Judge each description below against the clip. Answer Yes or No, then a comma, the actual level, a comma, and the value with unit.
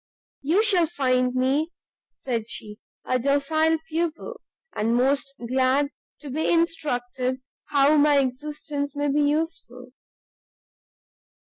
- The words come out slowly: Yes, slow, 110 wpm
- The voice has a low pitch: No, very high, 280 Hz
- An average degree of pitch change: Yes, average, 3.3 semitones